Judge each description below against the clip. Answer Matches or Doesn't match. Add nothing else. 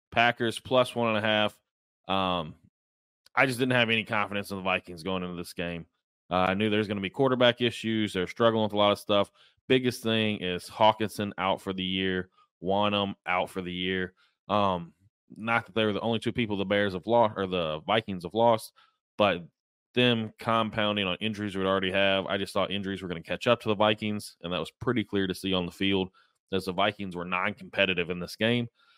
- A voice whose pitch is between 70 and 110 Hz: Matches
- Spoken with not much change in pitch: Doesn't match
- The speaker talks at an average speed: Doesn't match